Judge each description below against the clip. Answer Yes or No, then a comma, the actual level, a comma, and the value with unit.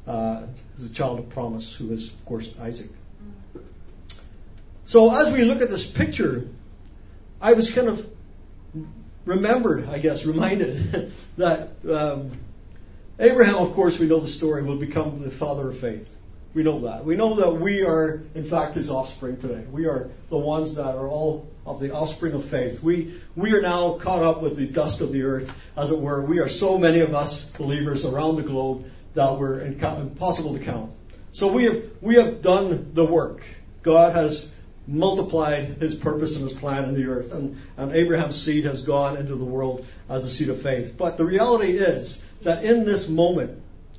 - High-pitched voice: No, medium, 145 Hz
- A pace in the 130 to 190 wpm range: Yes, average, 185 wpm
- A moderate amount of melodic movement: Yes, average, 4.8 semitones